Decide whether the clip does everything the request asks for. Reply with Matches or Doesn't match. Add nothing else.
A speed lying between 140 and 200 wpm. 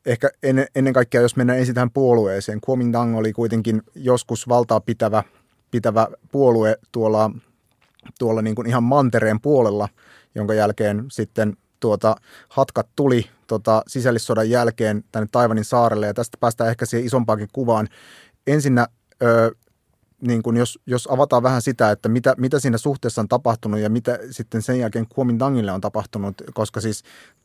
Matches